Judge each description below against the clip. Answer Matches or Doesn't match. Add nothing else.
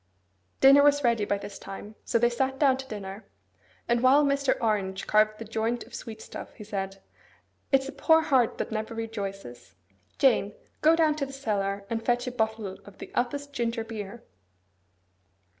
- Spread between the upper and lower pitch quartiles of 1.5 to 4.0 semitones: Doesn't match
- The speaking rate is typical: Matches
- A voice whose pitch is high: Matches